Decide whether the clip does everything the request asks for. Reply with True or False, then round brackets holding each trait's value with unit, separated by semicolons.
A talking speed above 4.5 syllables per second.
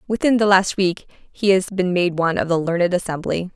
True (5.6 syllables/s)